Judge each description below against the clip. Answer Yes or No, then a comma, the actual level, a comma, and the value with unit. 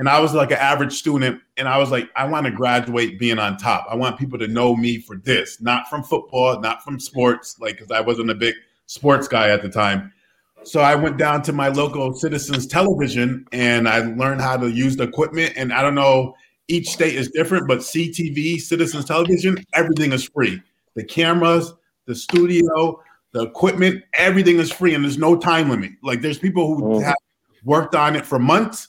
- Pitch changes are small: No, average, 4.8 semitones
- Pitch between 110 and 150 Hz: Yes, medium, 140 Hz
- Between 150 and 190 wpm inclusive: No, fast, 205 wpm